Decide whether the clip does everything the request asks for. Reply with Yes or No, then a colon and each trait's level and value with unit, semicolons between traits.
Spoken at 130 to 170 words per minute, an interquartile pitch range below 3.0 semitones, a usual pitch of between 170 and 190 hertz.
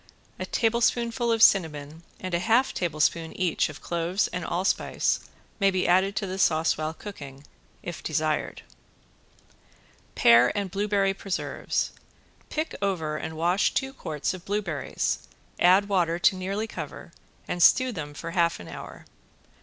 No: average, 140 wpm; average, 3.8 semitones; medium, 185 Hz